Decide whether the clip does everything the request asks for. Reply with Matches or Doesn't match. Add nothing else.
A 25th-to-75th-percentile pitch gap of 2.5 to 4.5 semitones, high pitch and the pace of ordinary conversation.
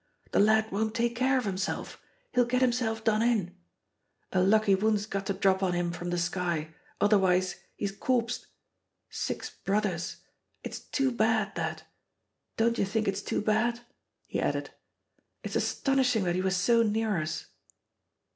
Matches